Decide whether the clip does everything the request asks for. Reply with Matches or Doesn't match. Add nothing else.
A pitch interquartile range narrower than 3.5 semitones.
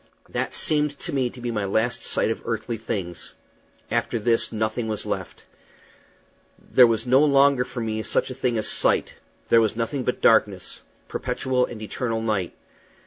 Matches